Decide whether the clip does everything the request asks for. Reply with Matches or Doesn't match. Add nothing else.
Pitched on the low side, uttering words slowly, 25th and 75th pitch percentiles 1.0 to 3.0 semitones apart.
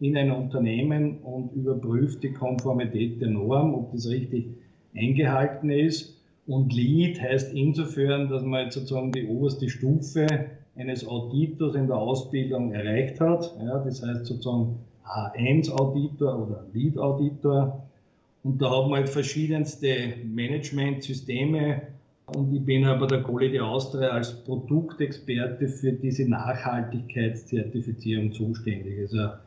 Matches